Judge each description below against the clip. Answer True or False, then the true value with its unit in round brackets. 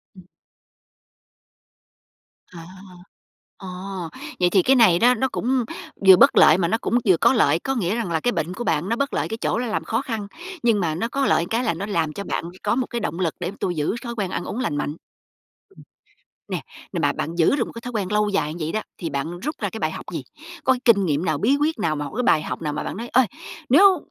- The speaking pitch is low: False (200 Hz)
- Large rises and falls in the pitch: True (6.1 semitones)